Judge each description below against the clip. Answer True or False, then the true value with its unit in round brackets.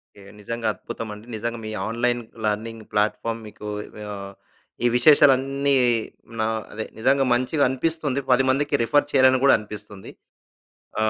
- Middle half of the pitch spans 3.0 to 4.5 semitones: True (4.0 semitones)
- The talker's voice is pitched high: False (120 Hz)